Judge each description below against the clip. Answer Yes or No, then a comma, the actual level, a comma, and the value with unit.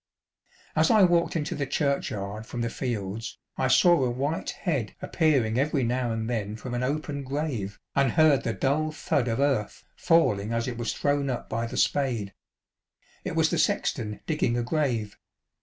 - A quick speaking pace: No, average, 175 wpm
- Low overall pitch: Yes, low, 125 Hz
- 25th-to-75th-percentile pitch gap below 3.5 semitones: No, average, 4.3 semitones